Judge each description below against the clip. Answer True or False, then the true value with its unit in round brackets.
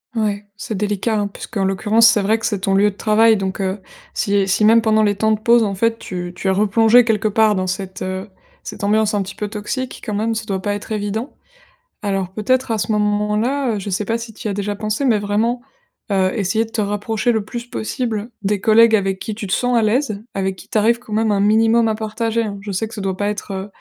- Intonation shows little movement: True (1.9 semitones)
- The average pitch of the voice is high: True (210 Hz)